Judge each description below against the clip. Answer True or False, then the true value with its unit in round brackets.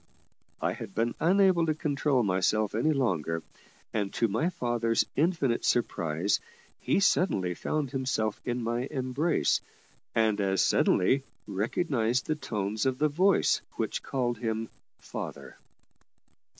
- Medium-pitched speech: False (120 Hz)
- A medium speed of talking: False (125 wpm)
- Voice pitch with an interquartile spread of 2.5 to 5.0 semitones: False (5.6 semitones)